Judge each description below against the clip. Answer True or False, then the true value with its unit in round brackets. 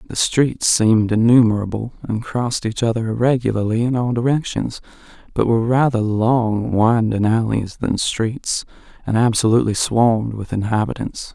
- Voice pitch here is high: False (115 Hz)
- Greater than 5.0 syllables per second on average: False (4.9 syllables/s)